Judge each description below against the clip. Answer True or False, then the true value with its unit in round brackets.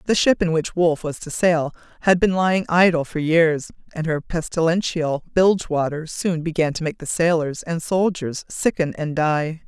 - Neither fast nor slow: True (185 wpm)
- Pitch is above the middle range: False (165 Hz)